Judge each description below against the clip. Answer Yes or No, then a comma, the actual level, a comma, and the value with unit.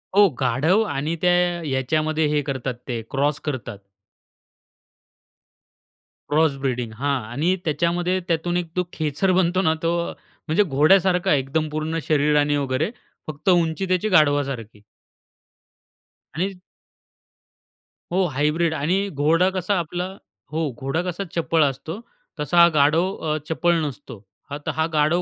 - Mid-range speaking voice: Yes, medium, 155 Hz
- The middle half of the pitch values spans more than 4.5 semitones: No, average, 3.4 semitones